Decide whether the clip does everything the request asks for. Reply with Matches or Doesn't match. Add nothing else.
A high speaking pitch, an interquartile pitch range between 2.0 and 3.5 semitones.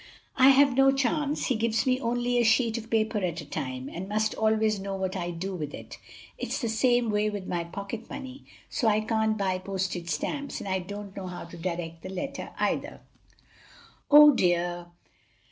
Doesn't match